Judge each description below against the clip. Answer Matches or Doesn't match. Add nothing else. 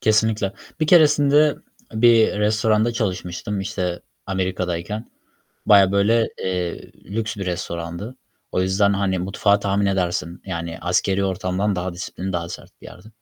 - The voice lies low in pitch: Matches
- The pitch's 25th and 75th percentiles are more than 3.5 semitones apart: Doesn't match